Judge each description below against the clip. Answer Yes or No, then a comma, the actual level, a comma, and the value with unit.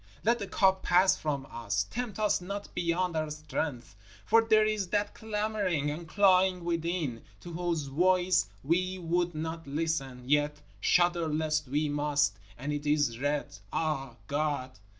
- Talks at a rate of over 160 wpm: No, average, 150 wpm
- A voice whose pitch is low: No, medium, 165 Hz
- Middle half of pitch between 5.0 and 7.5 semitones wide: No, average, 4.0 semitones